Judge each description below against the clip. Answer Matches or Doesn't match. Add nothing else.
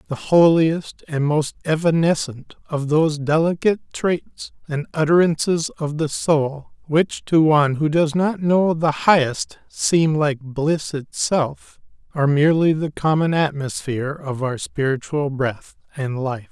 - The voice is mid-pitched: Matches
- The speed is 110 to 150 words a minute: Matches